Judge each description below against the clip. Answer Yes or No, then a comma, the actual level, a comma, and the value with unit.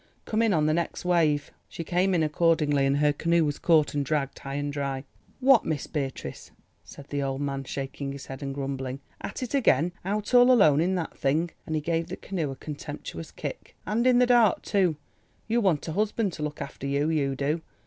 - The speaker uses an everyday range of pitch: Yes, average, 4.4 semitones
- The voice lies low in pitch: No, medium, 155 Hz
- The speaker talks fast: Yes, fast, 215 wpm